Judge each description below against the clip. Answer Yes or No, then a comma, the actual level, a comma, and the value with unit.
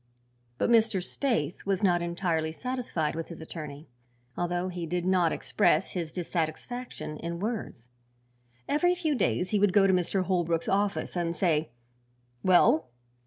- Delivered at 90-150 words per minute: Yes, average, 145 wpm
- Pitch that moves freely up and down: No, average, 3.5 semitones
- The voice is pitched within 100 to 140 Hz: No, medium, 180 Hz